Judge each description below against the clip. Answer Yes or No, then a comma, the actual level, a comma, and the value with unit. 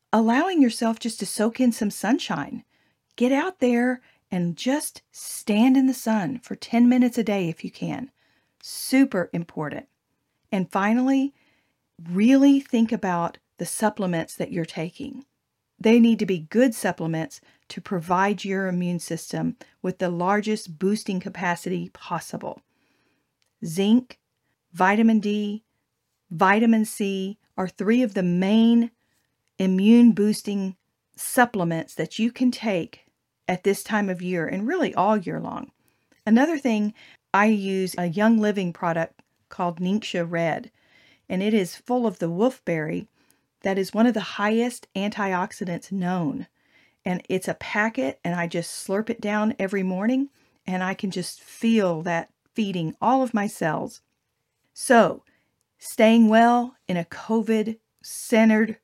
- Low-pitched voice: No, high, 205 Hz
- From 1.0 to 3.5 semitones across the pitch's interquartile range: No, average, 4.3 semitones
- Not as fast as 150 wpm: Yes, average, 140 wpm